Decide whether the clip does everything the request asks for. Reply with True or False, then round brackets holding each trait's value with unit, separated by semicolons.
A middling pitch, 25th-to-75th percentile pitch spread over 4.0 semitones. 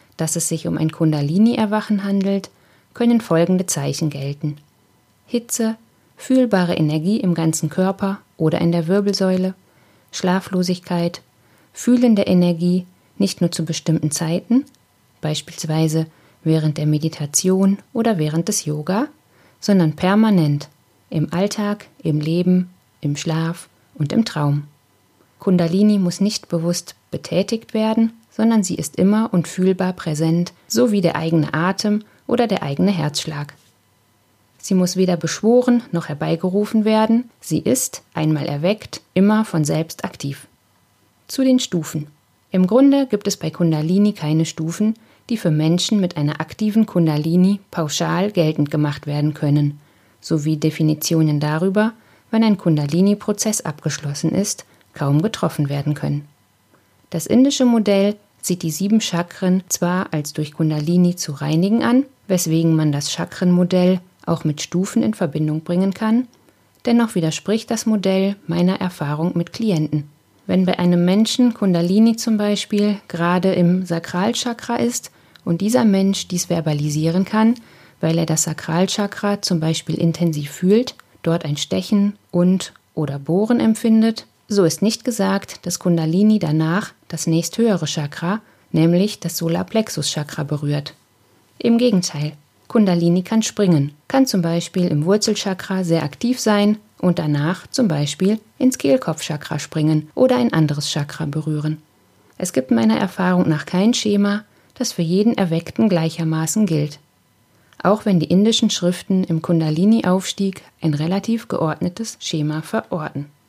True (175 Hz; 4.8 semitones)